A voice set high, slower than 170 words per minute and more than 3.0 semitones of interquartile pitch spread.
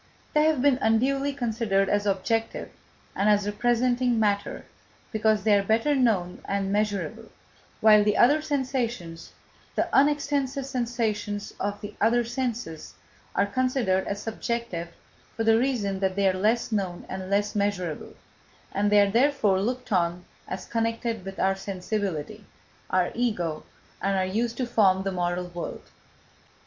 Yes: high, 210 Hz; average, 145 wpm; average, 3.7 semitones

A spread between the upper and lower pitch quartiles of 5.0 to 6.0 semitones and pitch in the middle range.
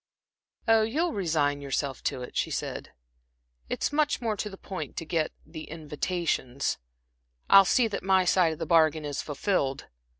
Yes: wide, 5.5 semitones; medium, 165 Hz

